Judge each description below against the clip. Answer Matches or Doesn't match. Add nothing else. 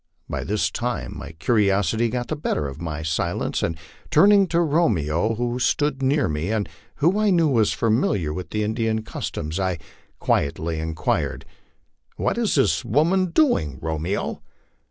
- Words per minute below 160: Matches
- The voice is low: Matches